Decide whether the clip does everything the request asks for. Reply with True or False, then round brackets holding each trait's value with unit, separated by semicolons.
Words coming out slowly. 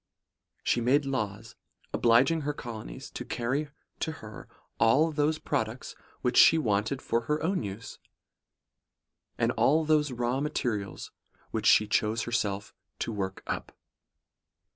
True (130 wpm)